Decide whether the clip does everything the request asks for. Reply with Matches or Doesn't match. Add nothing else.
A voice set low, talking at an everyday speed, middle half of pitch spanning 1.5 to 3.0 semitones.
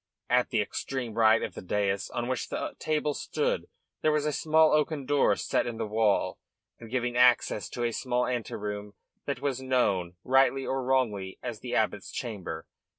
Doesn't match